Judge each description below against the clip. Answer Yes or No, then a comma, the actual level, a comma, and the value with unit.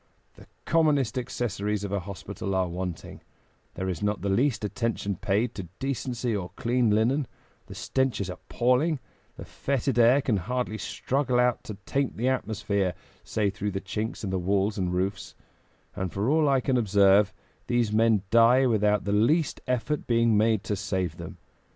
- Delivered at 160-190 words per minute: Yes, average, 170 wpm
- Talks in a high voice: No, low, 110 Hz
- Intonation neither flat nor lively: Yes, average, 4.0 semitones